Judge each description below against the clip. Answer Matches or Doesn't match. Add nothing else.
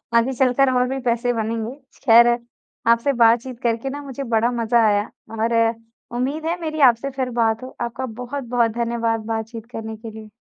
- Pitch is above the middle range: Matches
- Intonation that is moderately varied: Doesn't match